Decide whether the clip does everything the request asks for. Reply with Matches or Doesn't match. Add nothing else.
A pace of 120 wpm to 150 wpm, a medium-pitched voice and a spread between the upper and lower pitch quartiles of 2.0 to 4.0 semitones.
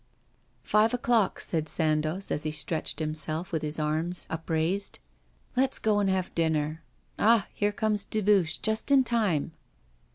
Doesn't match